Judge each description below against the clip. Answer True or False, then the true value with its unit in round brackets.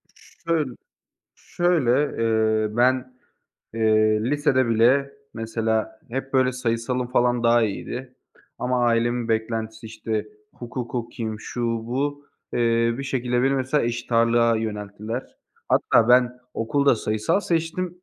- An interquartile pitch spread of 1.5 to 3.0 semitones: True (2.6 semitones)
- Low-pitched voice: True (120 Hz)